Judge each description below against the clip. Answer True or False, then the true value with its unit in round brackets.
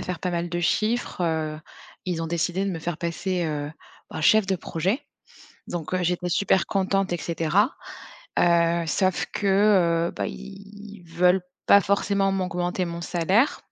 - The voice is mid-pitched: True (180 Hz)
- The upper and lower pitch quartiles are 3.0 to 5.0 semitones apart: False (2.6 semitones)